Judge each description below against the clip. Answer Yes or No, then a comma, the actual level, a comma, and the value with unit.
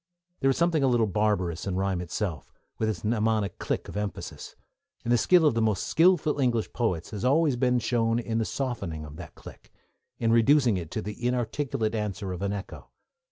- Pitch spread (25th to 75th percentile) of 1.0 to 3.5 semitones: No, average, 4.2 semitones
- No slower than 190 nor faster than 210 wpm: Yes, average, 200 wpm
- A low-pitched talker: Yes, low, 110 Hz